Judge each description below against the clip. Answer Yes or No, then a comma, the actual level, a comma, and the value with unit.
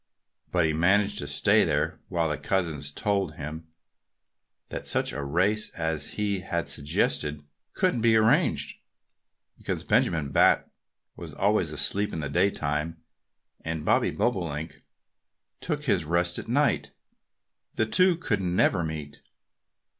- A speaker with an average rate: No, slow, 130 wpm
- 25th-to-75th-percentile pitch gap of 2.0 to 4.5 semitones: No, average, 4.9 semitones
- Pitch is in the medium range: No, very low, 85 Hz